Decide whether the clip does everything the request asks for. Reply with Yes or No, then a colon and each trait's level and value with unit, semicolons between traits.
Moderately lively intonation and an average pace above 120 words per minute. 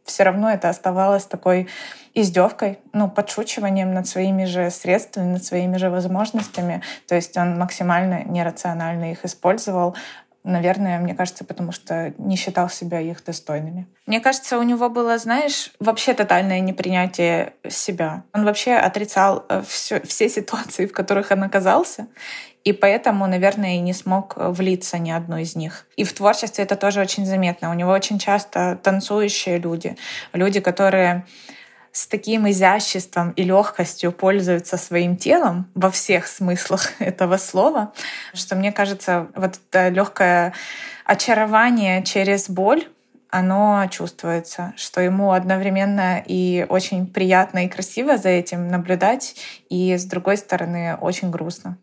No: narrow, 2.2 semitones; average, 140 wpm